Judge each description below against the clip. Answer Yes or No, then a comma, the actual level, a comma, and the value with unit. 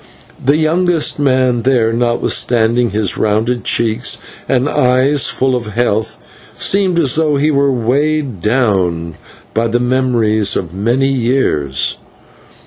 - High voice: No, low, 125 Hz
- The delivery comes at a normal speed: No, slow, 125 wpm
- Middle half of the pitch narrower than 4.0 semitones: Yes, average, 3.6 semitones